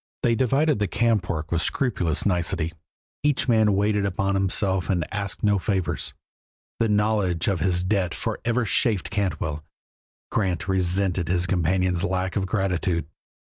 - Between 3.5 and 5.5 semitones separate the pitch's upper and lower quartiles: No, average, 3.0 semitones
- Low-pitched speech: Yes, very low, 95 Hz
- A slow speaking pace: No, average, 145 wpm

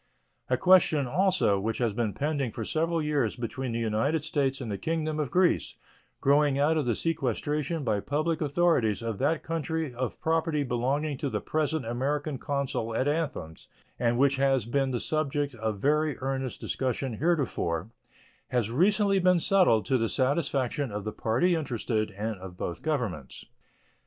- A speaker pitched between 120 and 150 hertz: Yes, medium, 140 Hz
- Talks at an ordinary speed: Yes, average, 165 wpm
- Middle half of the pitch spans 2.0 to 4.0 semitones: No, average, 4.9 semitones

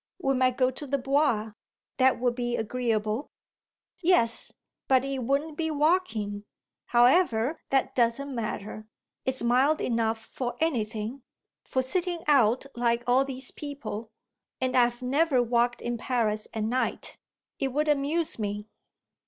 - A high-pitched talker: Yes, very high, 255 Hz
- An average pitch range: Yes, average, 3.3 semitones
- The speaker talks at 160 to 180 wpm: No, slow, 135 wpm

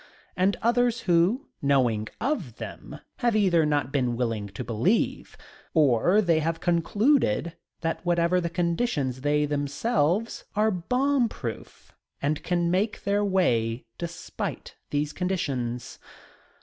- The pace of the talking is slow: Yes, slow, 125 wpm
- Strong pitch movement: Yes, wide, 6.5 semitones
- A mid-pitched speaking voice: Yes, medium, 170 Hz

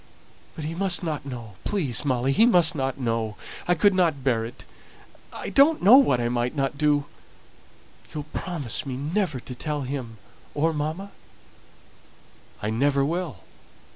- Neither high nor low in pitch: Yes, medium, 145 Hz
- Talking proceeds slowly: No, average, 150 wpm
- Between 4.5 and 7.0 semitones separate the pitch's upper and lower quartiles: Yes, wide, 5.5 semitones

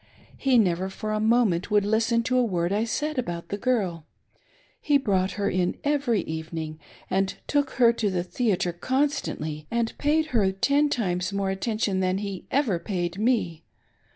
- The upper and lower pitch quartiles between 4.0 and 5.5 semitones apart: Yes, average, 5.1 semitones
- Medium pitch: No, high, 205 Hz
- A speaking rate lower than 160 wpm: No, average, 175 wpm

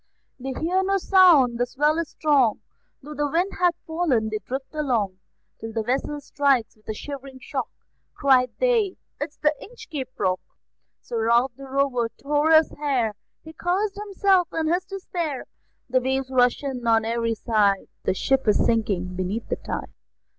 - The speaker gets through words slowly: No, average, 170 wpm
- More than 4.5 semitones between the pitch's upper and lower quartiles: Yes, wide, 5.5 semitones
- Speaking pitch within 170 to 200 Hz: No, very high, 270 Hz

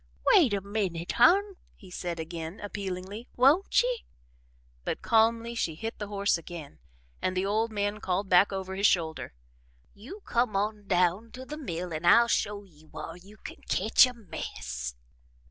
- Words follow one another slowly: No, average, 165 wpm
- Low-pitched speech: No, high, 200 Hz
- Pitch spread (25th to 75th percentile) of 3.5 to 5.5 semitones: Yes, average, 4.3 semitones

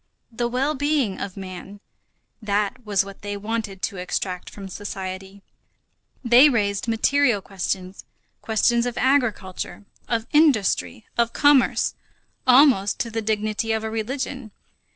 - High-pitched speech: Yes, high, 215 Hz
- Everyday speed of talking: No, slow, 130 wpm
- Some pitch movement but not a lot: Yes, average, 3.8 semitones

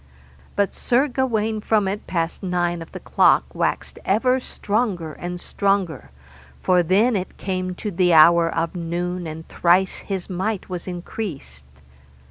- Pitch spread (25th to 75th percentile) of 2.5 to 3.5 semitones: Yes, average, 3.2 semitones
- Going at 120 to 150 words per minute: Yes, average, 145 wpm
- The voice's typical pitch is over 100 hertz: Yes, medium, 185 Hz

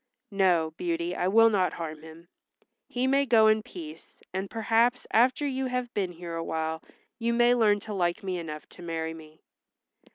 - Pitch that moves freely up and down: Yes, wide, 5.7 semitones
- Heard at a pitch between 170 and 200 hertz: Yes, high, 190 Hz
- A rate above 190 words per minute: No, average, 175 wpm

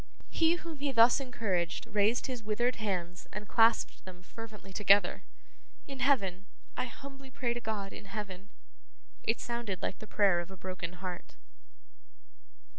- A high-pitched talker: Yes, high, 210 Hz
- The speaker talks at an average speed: Yes, average, 150 wpm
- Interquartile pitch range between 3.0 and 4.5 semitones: Yes, average, 4.2 semitones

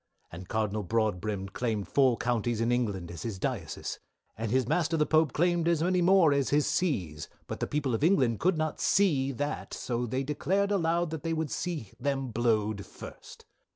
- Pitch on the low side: Yes, low, 130 Hz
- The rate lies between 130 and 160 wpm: No, average, 185 wpm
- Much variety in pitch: Yes, wide, 6.7 semitones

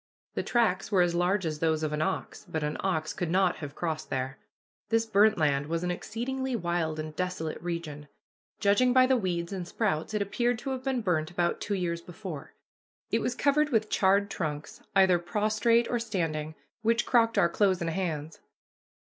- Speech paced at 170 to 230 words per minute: Yes, average, 190 wpm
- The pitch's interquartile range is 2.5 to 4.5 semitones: No, wide, 5.4 semitones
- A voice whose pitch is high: No, medium, 180 Hz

